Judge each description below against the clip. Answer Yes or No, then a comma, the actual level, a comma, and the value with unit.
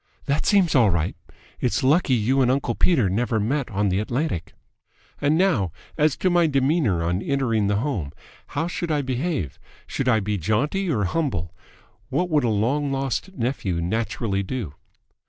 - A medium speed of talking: Yes, average, 170 wpm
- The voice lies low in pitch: Yes, low, 125 Hz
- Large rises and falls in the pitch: Yes, wide, 6.4 semitones